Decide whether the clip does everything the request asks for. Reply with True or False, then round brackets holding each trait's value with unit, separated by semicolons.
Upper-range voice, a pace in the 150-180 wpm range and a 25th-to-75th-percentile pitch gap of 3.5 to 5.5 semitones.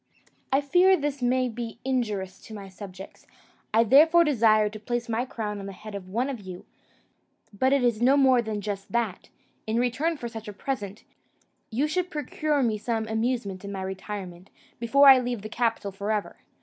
False (230 Hz; 190 wpm; 4.2 semitones)